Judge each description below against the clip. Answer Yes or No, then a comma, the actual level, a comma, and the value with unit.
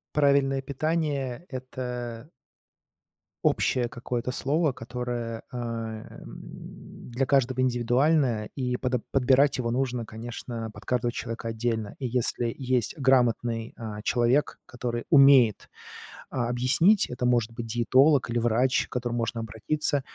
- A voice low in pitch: Yes, low, 125 Hz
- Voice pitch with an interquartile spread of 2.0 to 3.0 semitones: Yes, narrow, 2.4 semitones